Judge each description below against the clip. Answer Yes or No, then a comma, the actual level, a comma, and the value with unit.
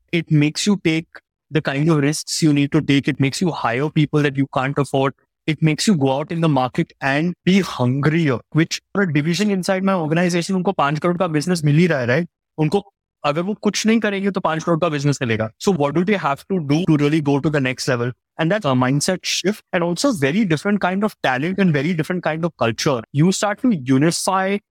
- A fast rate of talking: No, average, 190 wpm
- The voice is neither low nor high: Yes, medium, 160 Hz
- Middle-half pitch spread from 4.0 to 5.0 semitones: Yes, average, 4.7 semitones